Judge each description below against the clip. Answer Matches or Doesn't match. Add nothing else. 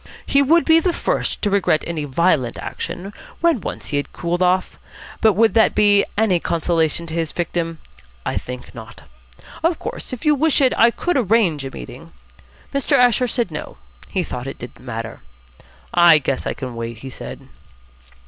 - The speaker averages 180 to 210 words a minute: Matches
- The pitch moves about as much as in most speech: Doesn't match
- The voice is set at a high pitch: Doesn't match